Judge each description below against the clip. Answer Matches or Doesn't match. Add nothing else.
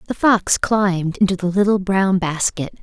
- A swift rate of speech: Doesn't match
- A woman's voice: Matches